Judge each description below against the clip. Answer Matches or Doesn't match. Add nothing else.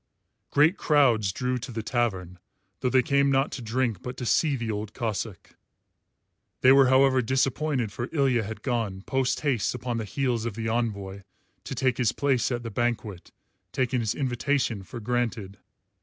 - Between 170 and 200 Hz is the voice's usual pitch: Doesn't match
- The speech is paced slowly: Doesn't match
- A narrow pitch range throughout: Doesn't match